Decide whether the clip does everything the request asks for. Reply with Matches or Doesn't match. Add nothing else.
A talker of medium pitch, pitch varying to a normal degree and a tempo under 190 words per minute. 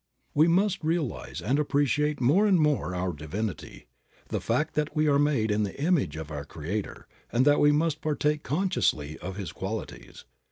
Doesn't match